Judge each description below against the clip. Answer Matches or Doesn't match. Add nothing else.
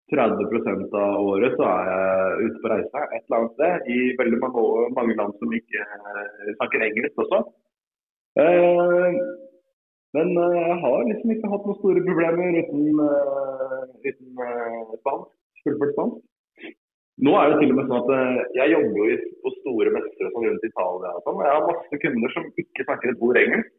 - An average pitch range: Doesn't match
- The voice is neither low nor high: Matches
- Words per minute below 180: Matches